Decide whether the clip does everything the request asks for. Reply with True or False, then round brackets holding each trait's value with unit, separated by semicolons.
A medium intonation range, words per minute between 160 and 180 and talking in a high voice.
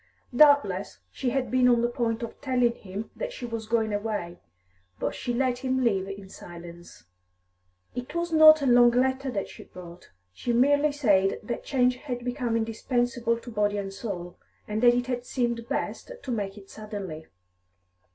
True (3.7 semitones; 175 wpm; 235 Hz)